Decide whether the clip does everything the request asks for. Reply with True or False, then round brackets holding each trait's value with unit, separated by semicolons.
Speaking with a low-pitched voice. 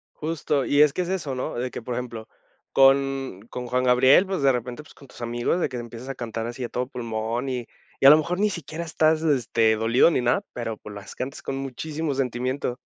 True (130 Hz)